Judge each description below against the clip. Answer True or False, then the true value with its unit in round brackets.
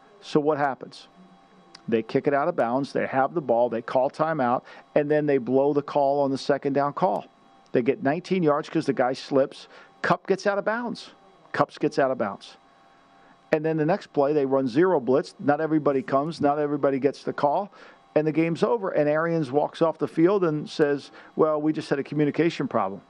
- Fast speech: True (210 wpm)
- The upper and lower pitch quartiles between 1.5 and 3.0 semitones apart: True (2.4 semitones)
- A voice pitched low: False (145 Hz)